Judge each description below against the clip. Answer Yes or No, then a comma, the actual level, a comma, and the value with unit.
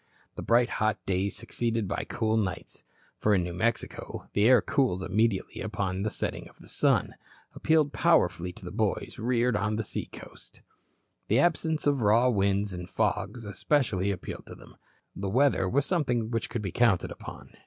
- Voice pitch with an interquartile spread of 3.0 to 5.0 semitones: Yes, average, 3.9 semitones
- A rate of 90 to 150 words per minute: No, average, 170 wpm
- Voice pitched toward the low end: Yes, low, 110 Hz